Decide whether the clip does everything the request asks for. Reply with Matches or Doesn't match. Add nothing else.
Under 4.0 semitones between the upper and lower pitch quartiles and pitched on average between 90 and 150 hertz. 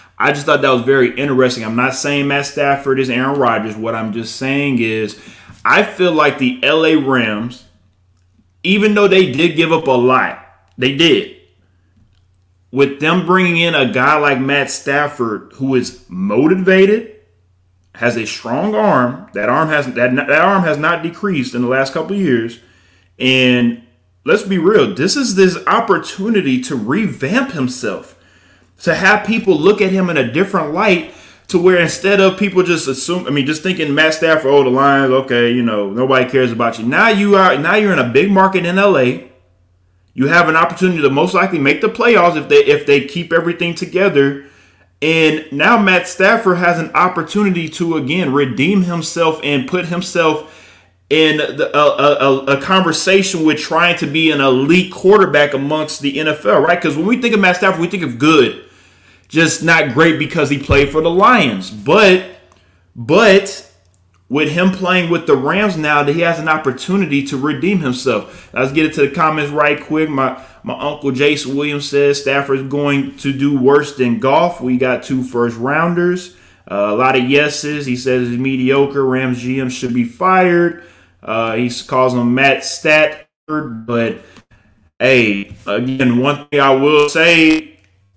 Doesn't match